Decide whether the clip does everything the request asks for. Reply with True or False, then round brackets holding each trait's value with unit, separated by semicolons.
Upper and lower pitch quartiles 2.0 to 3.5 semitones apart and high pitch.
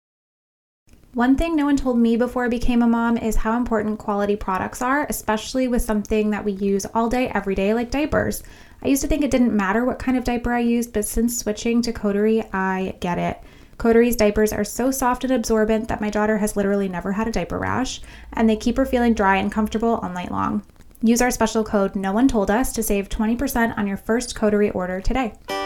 True (2.8 semitones; 225 Hz)